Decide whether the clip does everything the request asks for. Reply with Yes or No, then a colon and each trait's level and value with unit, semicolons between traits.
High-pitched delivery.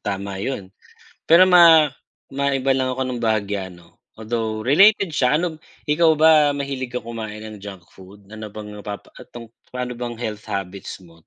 No: low, 115 Hz